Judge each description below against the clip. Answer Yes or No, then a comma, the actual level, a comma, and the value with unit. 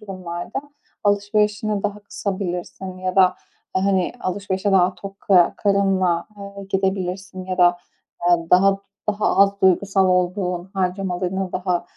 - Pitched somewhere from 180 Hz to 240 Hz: Yes, high, 190 Hz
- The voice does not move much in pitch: Yes, narrow, 1.5 semitones